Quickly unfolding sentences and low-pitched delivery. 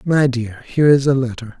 Yes: fast, 225 wpm; low, 130 Hz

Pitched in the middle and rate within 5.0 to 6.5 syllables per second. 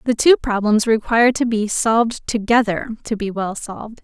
No: high, 225 Hz; 5.1 syllables/s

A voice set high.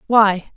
Yes: high, 205 Hz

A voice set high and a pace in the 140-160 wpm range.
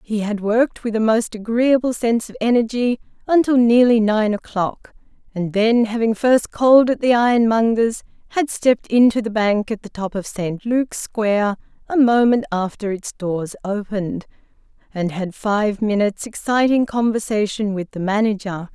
Yes: high, 220 Hz; average, 155 wpm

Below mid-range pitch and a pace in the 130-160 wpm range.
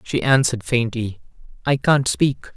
Yes: low, 120 Hz; average, 140 wpm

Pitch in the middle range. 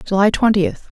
No: high, 205 Hz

